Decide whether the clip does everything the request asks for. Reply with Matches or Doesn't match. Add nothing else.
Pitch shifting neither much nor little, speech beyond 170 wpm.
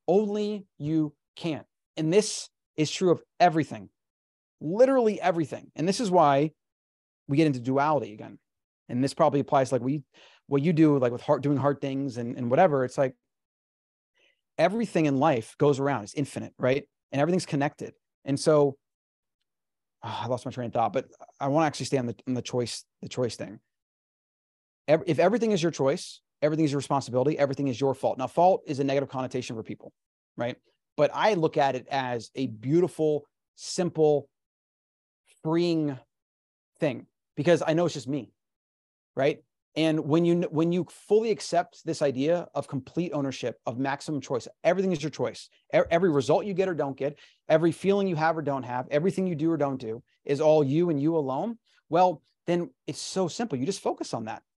Matches